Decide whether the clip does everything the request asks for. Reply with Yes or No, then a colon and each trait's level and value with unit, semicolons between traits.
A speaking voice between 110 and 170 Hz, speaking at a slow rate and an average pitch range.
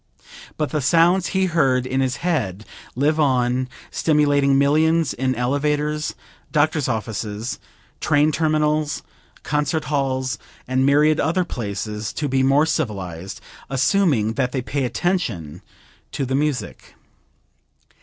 Yes: medium, 140 Hz; slow, 120 wpm; average, 3.4 semitones